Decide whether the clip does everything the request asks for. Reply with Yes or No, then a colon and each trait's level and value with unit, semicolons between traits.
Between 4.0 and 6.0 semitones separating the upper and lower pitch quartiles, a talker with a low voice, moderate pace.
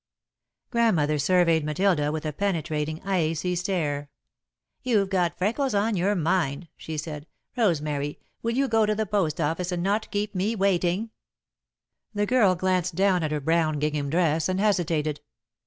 No: average, 4.6 semitones; medium, 180 Hz; average, 150 wpm